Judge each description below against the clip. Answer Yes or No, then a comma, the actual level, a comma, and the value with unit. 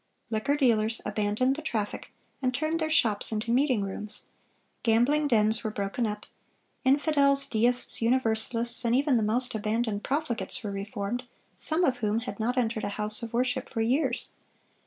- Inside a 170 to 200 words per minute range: No, average, 160 wpm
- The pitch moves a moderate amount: Yes, average, 3.3 semitones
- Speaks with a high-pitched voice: Yes, high, 235 Hz